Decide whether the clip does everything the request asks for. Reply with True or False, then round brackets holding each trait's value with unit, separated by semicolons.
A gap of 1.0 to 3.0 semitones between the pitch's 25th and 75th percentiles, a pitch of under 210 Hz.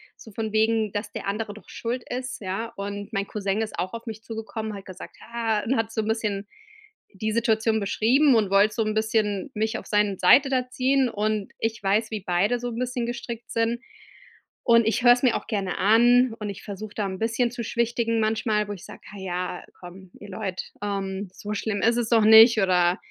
False (2.4 semitones; 220 Hz)